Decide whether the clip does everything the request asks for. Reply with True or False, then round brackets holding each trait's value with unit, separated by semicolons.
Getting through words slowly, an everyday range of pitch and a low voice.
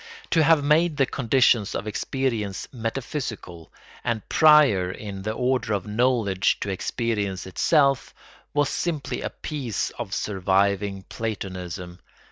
False (120 wpm; 5.7 semitones; 110 Hz)